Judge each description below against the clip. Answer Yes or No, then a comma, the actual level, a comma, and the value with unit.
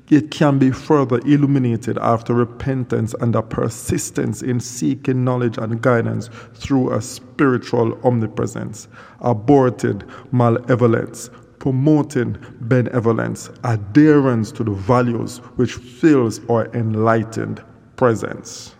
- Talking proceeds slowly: Yes, slow, 100 wpm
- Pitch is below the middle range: Yes, low, 120 Hz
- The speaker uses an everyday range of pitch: No, narrow, 2.0 semitones